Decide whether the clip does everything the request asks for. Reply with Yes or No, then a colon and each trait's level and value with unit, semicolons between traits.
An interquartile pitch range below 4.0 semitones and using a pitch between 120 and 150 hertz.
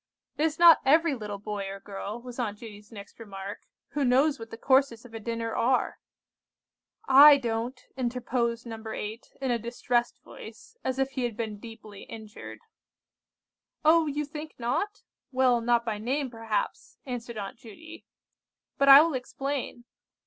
No: average, 3.4 semitones; high, 240 Hz